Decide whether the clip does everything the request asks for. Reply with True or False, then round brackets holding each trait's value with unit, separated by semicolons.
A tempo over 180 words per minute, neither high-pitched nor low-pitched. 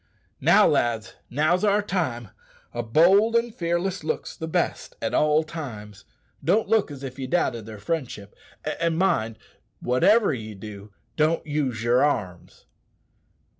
False (140 wpm; 150 Hz)